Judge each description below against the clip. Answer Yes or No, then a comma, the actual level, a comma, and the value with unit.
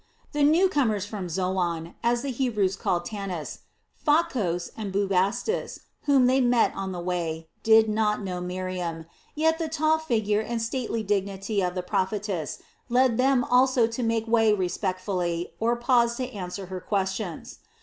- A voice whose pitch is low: No, high, 210 Hz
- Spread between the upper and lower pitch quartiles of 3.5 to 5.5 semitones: Yes, average, 4.8 semitones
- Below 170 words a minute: Yes, average, 160 wpm